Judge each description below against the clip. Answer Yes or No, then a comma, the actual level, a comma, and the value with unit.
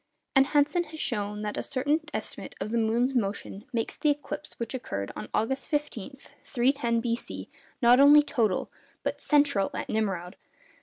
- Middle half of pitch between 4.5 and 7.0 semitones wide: Yes, average, 5.1 semitones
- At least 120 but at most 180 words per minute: Yes, average, 160 wpm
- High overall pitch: Yes, high, 240 Hz